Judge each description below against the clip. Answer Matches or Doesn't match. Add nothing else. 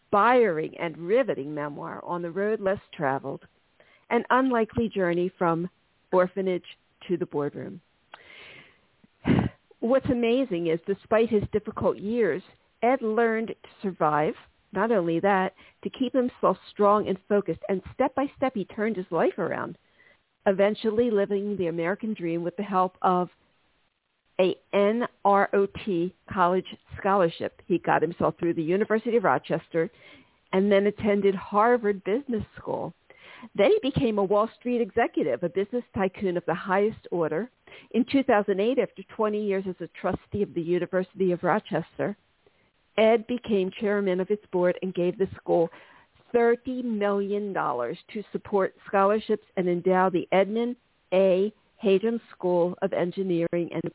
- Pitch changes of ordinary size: Matches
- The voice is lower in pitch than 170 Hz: Doesn't match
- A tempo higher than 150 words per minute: Doesn't match